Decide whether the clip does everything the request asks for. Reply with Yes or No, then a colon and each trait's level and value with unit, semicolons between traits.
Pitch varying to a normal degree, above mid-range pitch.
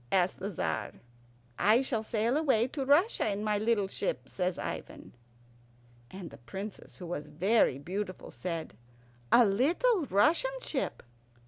No: wide, 6.4 semitones; high, 210 Hz